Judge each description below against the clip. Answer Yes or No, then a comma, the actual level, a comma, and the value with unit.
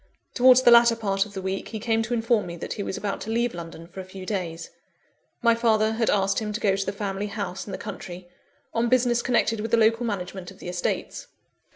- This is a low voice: No, high, 210 Hz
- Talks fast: Yes, fast, 240 wpm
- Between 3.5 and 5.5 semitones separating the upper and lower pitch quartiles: No, average, 3.1 semitones